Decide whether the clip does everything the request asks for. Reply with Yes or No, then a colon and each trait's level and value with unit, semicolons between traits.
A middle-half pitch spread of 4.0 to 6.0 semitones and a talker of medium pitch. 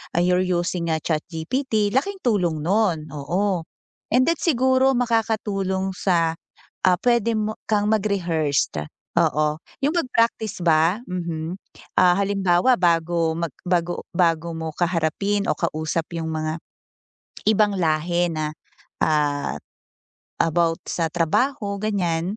Yes: average, 4.4 semitones; medium, 175 Hz